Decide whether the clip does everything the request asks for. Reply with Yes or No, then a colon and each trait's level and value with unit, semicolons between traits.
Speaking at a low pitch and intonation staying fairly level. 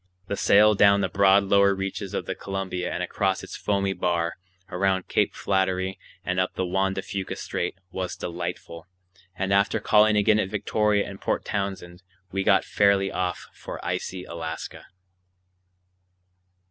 Yes: very low, 95 Hz; narrow, 1.5 semitones